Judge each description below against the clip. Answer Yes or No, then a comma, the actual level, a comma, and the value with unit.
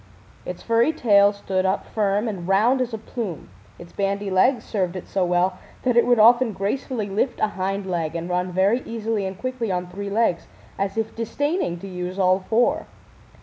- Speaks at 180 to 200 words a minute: Yes, average, 190 wpm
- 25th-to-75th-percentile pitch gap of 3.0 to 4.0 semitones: Yes, average, 3.6 semitones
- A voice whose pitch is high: Yes, high, 200 Hz